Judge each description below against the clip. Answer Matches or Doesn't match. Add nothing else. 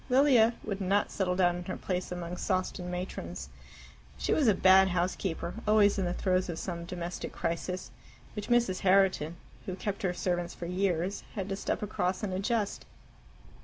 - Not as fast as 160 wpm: Doesn't match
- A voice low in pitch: Doesn't match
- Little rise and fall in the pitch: Matches